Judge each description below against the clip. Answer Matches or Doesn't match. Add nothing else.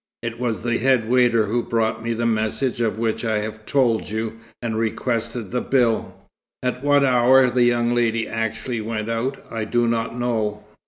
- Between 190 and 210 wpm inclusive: Doesn't match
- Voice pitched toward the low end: Matches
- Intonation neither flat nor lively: Doesn't match